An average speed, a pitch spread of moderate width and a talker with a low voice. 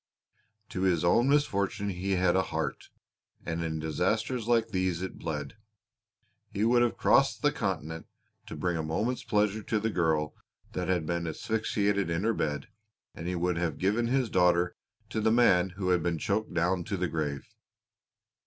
Yes: average, 175 wpm; average, 4.4 semitones; very low, 95 Hz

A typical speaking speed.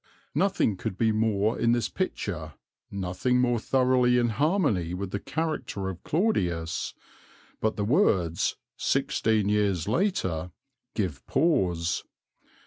No: slow, 125 wpm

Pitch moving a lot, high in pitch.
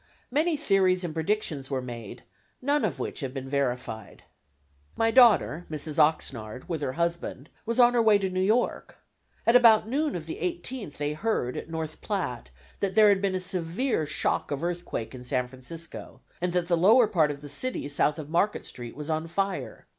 No: wide, 6.5 semitones; medium, 170 Hz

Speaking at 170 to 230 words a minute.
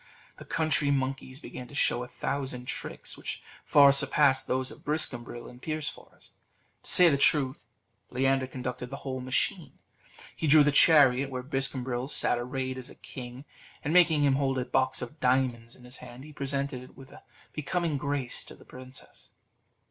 Yes: average, 175 wpm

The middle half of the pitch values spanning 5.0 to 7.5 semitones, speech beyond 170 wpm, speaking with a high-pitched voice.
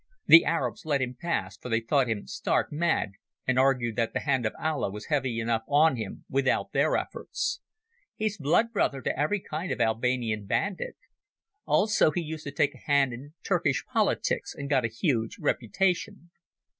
No: wide, 5.4 semitones; average, 180 wpm; medium, 140 Hz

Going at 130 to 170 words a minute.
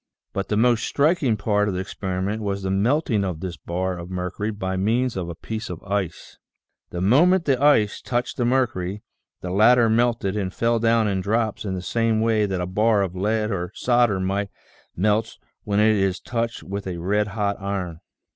No: average, 195 wpm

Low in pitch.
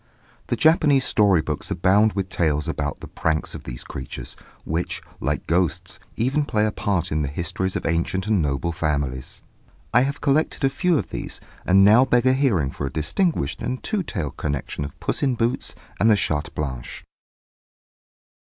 Yes: very low, 95 Hz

